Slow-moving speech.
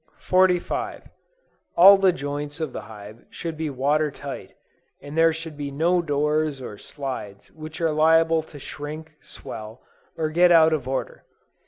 No: average, 155 wpm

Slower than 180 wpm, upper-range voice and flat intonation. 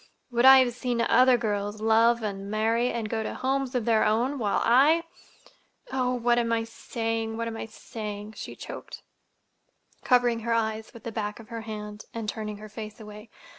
No: average, 185 wpm; high, 225 Hz; narrow, 2.0 semitones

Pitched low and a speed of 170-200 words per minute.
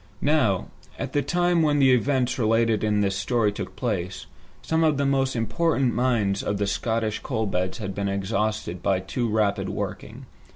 Yes: low, 110 Hz; average, 175 wpm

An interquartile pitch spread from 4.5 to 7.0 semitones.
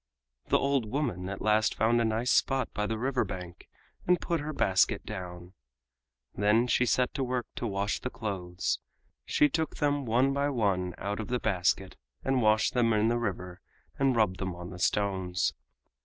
Yes: average, 5.1 semitones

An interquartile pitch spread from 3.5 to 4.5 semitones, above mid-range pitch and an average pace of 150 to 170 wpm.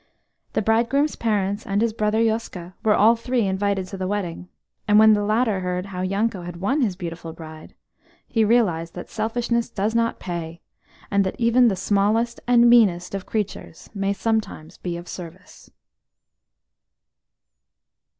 Yes: average, 3.8 semitones; high, 205 Hz; average, 155 wpm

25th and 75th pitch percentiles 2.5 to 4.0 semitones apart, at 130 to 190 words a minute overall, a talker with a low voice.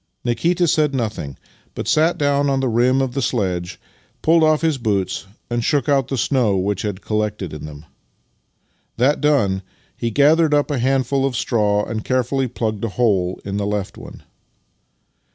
No: wide, 5.4 semitones; average, 170 wpm; low, 120 Hz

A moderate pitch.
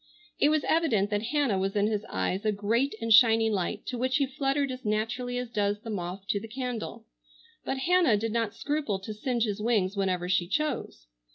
No: high, 225 Hz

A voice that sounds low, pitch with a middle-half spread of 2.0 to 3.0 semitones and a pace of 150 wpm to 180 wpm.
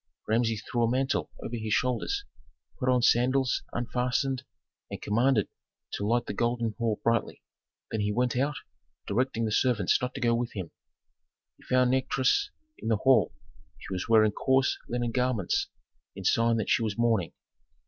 Yes: low, 120 Hz; narrow, 2.4 semitones; average, 165 wpm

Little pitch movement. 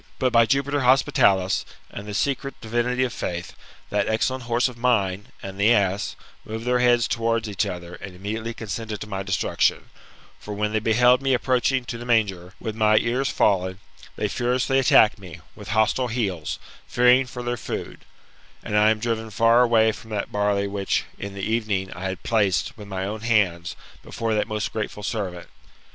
No: average, 3.3 semitones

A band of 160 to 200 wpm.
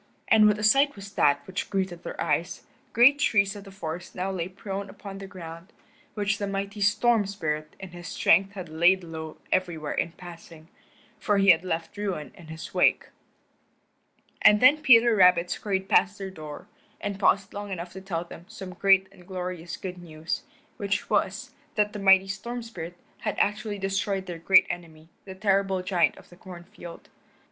Yes: average, 185 wpm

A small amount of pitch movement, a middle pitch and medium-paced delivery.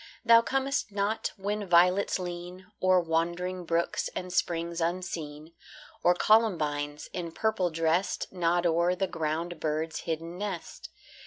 No: narrow, 2.1 semitones; medium, 175 Hz; slow, 130 wpm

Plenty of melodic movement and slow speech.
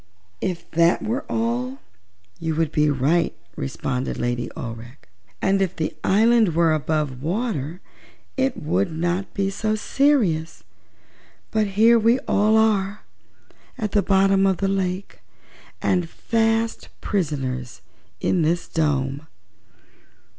Yes: wide, 5.9 semitones; slow, 120 wpm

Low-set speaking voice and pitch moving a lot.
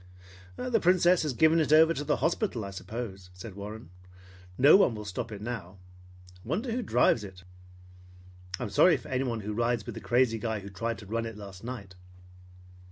Yes: low, 115 Hz; wide, 6.5 semitones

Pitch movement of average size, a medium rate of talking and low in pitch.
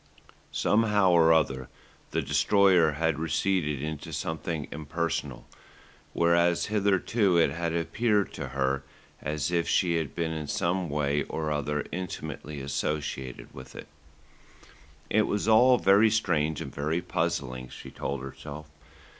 No: average, 4.0 semitones; slow, 130 wpm; very low, 80 Hz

